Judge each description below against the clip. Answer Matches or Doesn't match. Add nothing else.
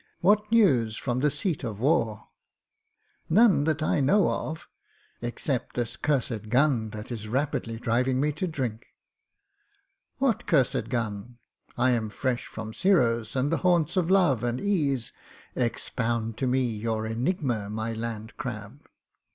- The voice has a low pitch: Matches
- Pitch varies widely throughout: Doesn't match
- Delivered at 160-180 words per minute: Doesn't match